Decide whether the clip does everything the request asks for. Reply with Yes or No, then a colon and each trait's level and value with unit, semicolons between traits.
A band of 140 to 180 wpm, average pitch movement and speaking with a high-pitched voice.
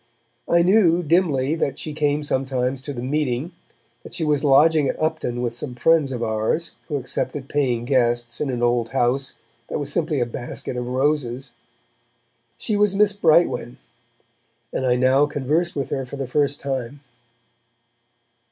No: average, 160 wpm; average, 3.7 semitones; medium, 140 Hz